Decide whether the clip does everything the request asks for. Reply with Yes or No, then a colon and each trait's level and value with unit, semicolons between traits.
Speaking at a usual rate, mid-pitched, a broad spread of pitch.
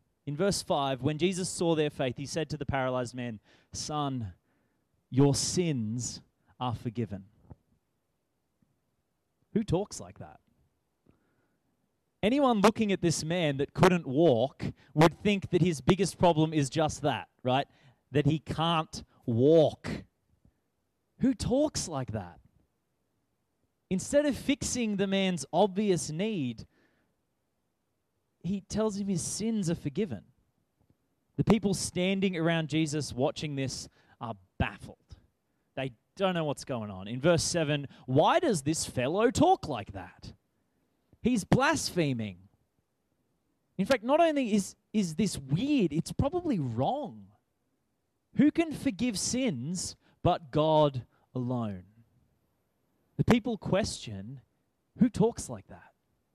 No: slow, 120 wpm; medium, 155 Hz; wide, 7.0 semitones